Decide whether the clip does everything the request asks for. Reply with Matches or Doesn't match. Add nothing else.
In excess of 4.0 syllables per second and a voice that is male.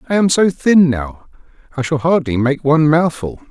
Matches